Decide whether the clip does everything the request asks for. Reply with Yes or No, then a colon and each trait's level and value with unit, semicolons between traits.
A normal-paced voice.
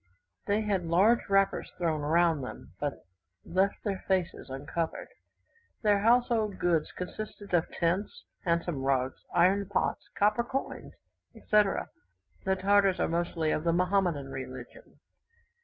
No: slow, 125 wpm